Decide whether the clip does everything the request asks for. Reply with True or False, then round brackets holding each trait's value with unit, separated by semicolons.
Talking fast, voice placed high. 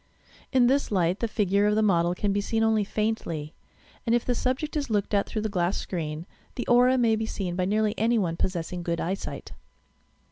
True (210 wpm; 210 Hz)